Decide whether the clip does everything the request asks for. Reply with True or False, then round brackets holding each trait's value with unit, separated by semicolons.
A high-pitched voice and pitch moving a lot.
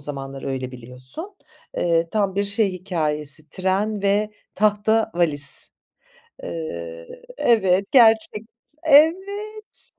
True (200 Hz; 6.5 semitones)